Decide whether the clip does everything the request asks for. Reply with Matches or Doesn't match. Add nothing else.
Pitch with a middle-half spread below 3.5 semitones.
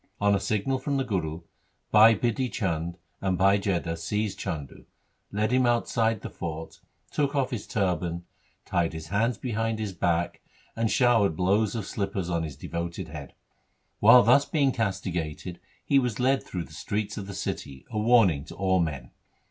Doesn't match